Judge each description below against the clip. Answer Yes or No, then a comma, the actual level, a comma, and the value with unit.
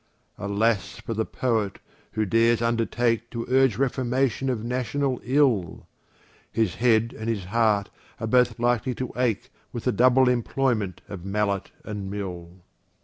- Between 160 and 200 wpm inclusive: No, average, 145 wpm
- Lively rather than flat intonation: No, average, 3.1 semitones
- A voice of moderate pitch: No, low, 115 Hz